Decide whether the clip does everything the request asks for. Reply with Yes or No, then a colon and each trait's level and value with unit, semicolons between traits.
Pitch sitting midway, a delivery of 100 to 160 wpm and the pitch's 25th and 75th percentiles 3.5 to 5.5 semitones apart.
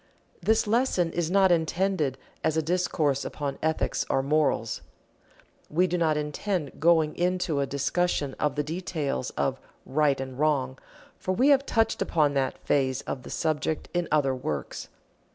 Yes: medium, 155 Hz; average, 155 wpm; average, 4.2 semitones